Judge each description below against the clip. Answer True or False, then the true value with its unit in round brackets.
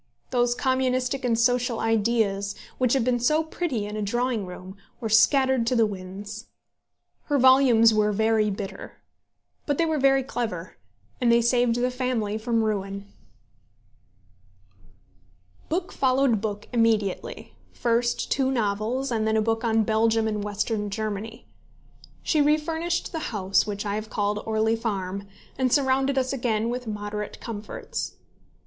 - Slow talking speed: False (145 wpm)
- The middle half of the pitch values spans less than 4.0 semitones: True (3.5 semitones)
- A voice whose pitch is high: True (230 Hz)